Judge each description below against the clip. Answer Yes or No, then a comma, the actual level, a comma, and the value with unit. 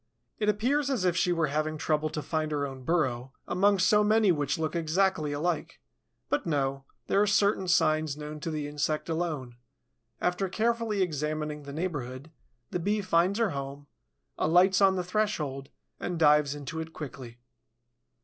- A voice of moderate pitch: Yes, medium, 160 Hz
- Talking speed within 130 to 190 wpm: Yes, average, 165 wpm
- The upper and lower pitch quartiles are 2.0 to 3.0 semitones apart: No, average, 4.3 semitones